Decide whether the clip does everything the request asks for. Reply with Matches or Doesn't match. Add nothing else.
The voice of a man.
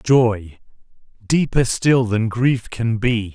Matches